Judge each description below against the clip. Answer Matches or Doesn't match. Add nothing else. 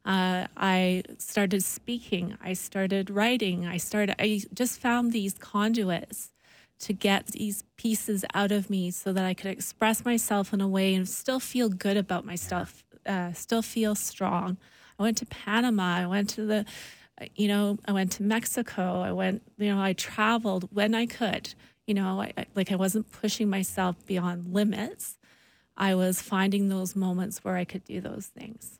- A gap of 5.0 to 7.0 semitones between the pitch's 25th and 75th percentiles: Doesn't match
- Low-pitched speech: Doesn't match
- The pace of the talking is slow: Doesn't match